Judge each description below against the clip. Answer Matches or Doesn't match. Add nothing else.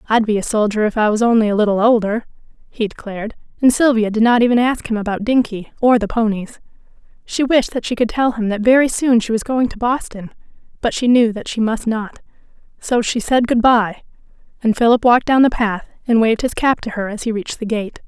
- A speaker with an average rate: Doesn't match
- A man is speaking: Doesn't match